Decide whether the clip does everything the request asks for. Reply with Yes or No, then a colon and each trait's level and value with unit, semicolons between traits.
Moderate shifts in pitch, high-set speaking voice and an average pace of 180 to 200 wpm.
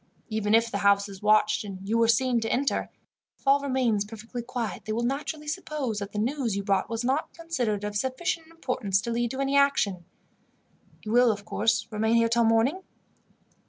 Yes: average, 4.0 semitones; high, 230 Hz; average, 195 wpm